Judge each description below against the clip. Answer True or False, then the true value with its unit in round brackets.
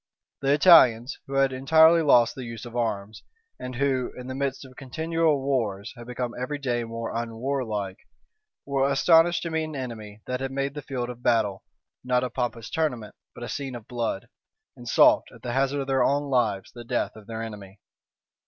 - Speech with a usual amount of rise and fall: True (3.0 semitones)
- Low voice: True (125 Hz)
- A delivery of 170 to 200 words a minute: True (190 wpm)